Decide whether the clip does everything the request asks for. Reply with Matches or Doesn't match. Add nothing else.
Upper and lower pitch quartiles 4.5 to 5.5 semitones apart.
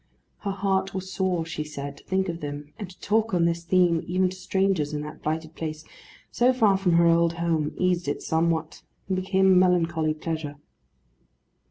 Doesn't match